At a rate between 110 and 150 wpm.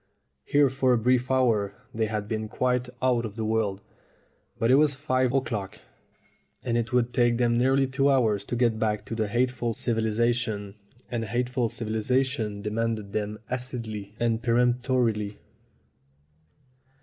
Yes: average, 145 wpm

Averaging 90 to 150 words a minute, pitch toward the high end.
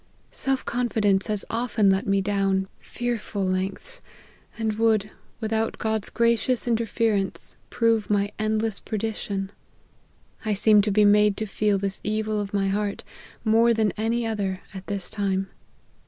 Yes: average, 140 wpm; high, 210 Hz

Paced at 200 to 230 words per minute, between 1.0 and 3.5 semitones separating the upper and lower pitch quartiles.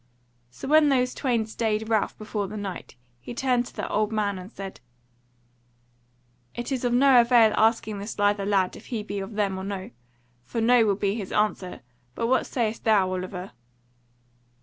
No: average, 180 wpm; average, 3.2 semitones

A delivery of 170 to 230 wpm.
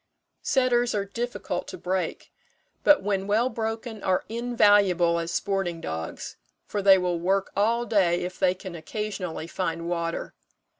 No: average, 145 wpm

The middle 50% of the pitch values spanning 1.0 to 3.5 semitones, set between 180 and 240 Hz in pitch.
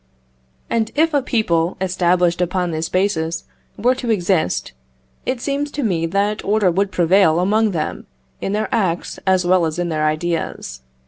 No: average, 4.2 semitones; medium, 185 Hz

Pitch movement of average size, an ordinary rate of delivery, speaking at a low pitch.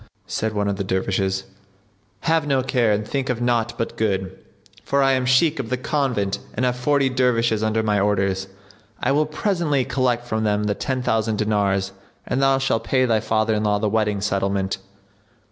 Yes: average, 4.1 semitones; average, 190 wpm; low, 110 Hz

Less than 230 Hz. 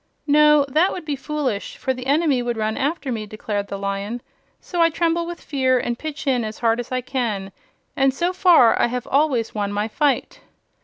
No: very high, 260 Hz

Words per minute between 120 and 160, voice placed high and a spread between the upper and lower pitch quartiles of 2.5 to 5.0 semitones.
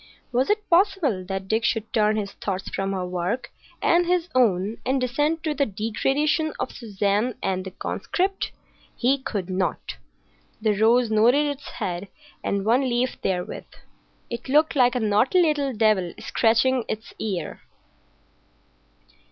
No: average, 145 wpm; high, 230 Hz; wide, 5.6 semitones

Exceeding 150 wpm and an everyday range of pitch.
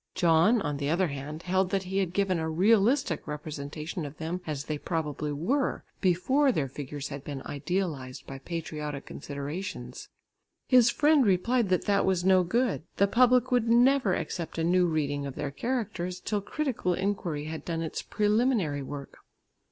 No: average, 165 wpm; wide, 5.7 semitones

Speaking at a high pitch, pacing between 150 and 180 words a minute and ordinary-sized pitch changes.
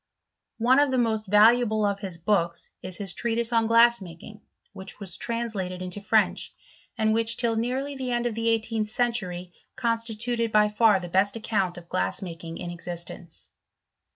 Yes: high, 215 Hz; average, 170 wpm; average, 4.0 semitones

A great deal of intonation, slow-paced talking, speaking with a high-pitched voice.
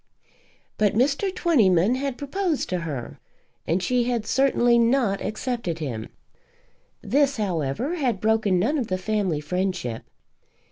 Yes: wide, 6.5 semitones; slow, 130 wpm; high, 220 Hz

